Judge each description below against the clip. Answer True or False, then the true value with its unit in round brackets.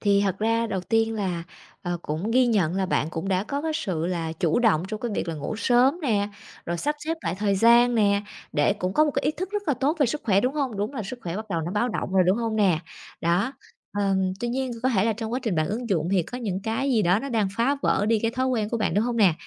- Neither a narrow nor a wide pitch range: True (4.6 semitones)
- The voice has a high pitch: True (215 Hz)